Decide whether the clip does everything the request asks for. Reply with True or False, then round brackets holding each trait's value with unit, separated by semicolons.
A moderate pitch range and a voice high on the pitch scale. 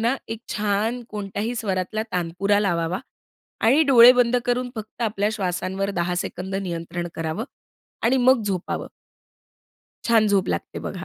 True (4.0 semitones; 205 Hz)